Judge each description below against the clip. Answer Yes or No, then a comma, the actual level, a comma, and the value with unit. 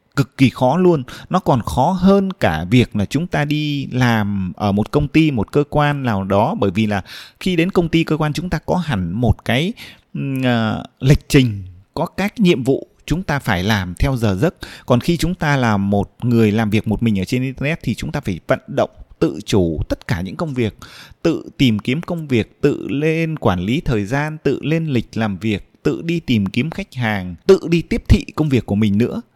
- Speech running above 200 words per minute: Yes, average, 225 wpm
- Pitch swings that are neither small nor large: No, wide, 6.6 semitones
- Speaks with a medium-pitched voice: No, low, 130 Hz